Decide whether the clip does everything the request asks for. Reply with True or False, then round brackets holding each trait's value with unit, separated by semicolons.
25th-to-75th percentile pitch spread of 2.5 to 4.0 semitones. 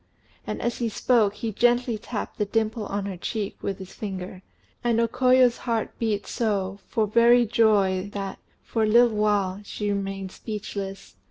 True (2.8 semitones)